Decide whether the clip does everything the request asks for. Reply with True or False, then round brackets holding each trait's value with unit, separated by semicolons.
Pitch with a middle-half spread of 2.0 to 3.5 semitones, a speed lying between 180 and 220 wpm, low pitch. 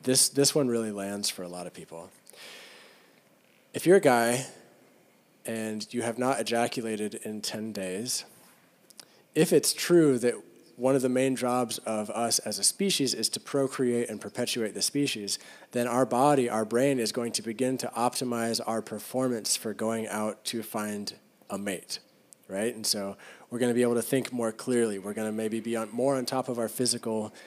True (2.9 semitones; 185 wpm; 120 Hz)